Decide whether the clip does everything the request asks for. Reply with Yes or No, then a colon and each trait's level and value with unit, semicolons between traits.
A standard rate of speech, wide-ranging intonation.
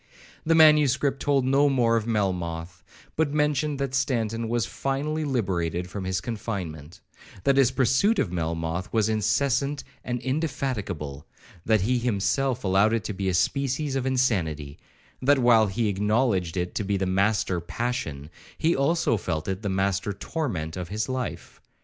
Yes: average, 150 wpm; wide, 6.4 semitones